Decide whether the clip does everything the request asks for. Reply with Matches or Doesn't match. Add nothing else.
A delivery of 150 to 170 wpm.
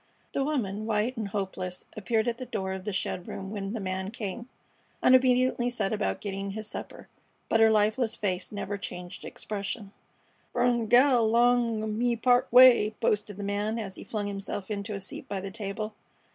Doesn't match